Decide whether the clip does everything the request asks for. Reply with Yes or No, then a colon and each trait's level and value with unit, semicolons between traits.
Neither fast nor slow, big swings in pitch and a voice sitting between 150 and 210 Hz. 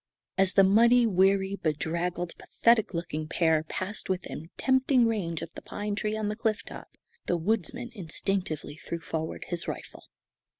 No: average, 155 wpm; average, 4.5 semitones; high, 190 Hz